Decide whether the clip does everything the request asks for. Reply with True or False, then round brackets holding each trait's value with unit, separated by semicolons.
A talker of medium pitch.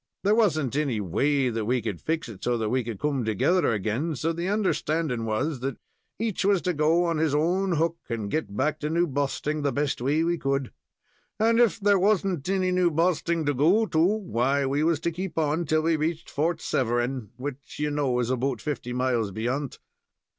True (150 Hz)